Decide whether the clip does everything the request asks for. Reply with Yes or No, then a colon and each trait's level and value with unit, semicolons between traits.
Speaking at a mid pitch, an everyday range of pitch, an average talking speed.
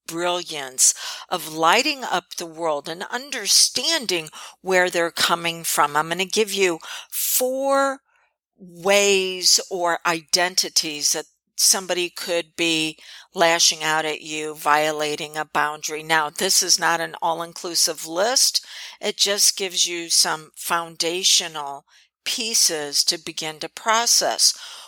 No: medium, 170 Hz; average, 3.2 semitones; slow, 125 wpm